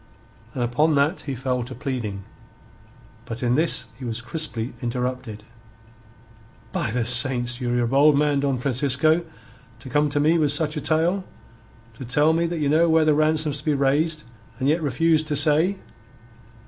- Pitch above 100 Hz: Yes, medium, 140 Hz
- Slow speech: No, average, 175 wpm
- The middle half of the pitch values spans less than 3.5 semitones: No, average, 3.8 semitones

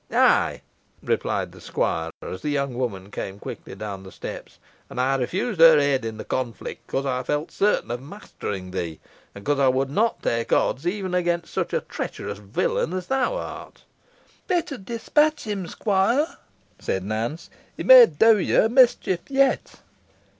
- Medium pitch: Yes, medium, 145 Hz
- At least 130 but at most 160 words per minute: No, average, 170 wpm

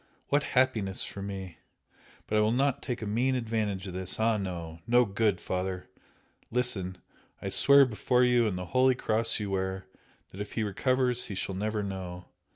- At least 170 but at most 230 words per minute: Yes, average, 180 wpm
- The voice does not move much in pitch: No, average, 4.6 semitones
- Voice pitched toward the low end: Yes, low, 105 Hz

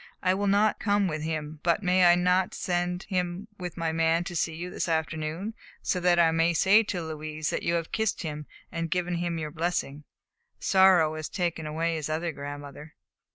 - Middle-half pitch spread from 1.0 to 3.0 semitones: Yes, narrow, 2.4 semitones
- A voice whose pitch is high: No, medium, 170 Hz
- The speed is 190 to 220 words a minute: Yes, average, 200 wpm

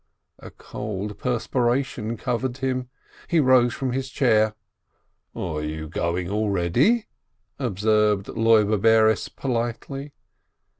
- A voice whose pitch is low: Yes, low, 115 Hz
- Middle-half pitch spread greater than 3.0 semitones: Yes, average, 3.7 semitones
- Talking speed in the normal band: No, slow, 100 wpm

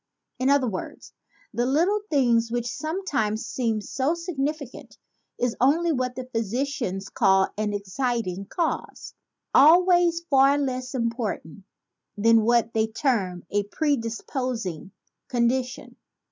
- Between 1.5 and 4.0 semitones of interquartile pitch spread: No, average, 4.4 semitones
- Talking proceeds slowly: Yes, slow, 115 wpm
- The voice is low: No, very high, 250 Hz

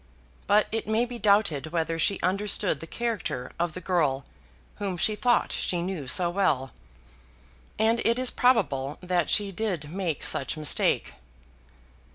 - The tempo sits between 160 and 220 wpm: No, average, 150 wpm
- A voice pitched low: No, medium, 185 Hz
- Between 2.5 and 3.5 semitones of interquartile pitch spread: No, average, 5.0 semitones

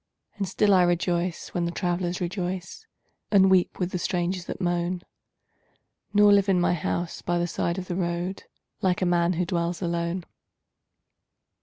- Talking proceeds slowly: No, average, 165 wpm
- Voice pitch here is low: No, medium, 175 Hz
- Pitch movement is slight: Yes, narrow, 1.4 semitones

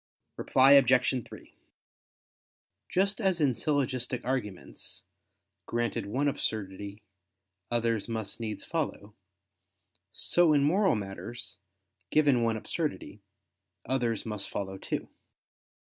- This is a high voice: No, low, 120 Hz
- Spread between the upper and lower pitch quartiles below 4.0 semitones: No, average, 4.9 semitones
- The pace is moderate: No, slow, 100 wpm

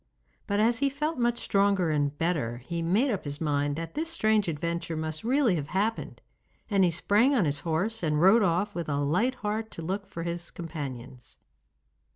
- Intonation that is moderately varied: No, wide, 5.7 semitones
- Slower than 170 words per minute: No, average, 190 wpm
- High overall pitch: No, medium, 175 Hz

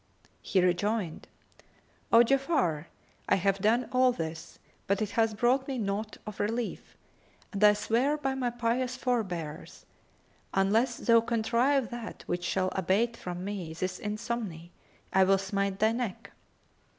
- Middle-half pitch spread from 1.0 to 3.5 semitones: No, average, 4.0 semitones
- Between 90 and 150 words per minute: Yes, average, 145 wpm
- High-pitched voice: Yes, high, 215 Hz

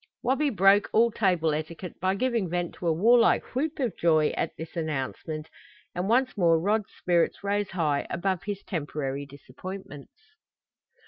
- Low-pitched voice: No, medium, 185 Hz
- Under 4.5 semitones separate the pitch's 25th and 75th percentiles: No, average, 5.0 semitones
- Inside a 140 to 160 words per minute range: Yes, average, 150 wpm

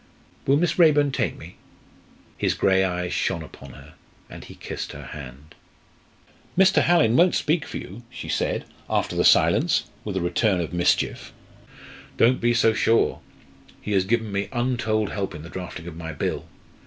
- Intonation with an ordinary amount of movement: No, wide, 6.1 semitones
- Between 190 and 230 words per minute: No, average, 170 wpm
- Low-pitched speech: Yes, low, 100 Hz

